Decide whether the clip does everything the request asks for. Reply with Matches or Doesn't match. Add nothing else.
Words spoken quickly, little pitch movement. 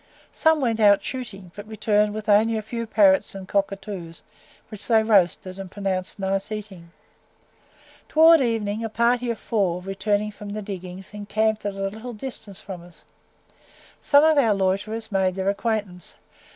Doesn't match